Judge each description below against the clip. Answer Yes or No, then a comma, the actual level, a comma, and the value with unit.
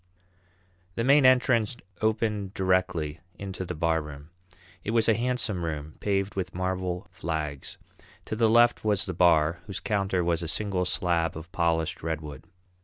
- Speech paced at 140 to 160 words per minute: Yes, average, 150 wpm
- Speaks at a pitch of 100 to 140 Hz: No, very low, 90 Hz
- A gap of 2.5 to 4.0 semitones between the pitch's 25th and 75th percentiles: No, average, 4.5 semitones